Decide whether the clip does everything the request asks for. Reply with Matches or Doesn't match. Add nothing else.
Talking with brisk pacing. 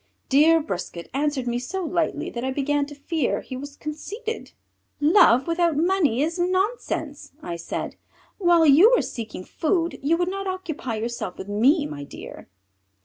Doesn't match